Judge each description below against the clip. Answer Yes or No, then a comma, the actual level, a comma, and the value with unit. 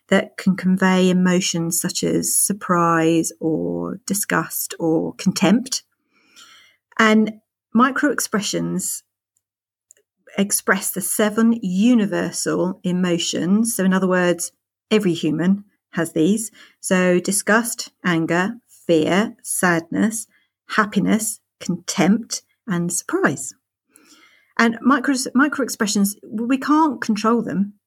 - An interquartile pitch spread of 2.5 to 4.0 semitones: No, average, 4.5 semitones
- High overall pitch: Yes, high, 195 Hz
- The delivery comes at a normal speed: No, slow, 90 wpm